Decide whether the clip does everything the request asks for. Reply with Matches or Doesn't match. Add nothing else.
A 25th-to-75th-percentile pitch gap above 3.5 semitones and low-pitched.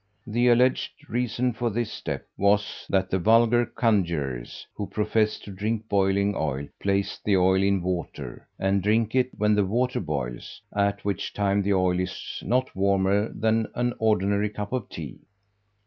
Doesn't match